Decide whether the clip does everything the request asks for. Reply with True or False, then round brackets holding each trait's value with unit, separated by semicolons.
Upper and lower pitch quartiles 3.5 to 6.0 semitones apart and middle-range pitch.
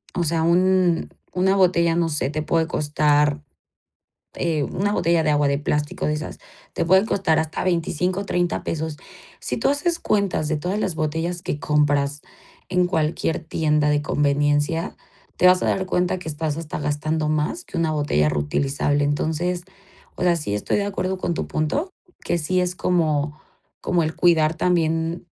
False (3.1 semitones; 160 Hz)